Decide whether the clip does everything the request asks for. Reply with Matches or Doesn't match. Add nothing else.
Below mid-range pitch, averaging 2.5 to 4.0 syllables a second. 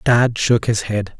Matches